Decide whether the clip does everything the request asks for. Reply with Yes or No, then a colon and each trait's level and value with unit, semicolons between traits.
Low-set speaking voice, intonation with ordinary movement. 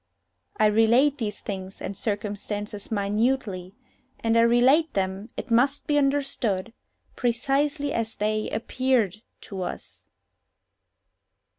No: high, 225 Hz; average, 4.4 semitones